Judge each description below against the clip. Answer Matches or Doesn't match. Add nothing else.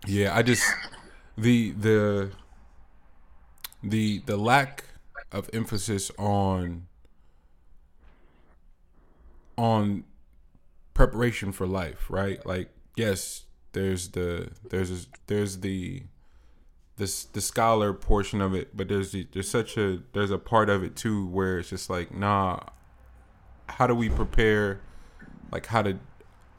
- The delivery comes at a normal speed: Doesn't match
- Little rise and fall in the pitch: Doesn't match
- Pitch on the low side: Matches